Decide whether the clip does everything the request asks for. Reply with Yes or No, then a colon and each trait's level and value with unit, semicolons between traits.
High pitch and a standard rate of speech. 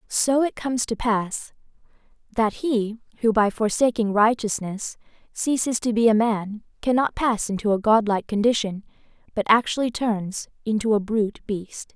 Yes: high, 220 Hz; average, 145 wpm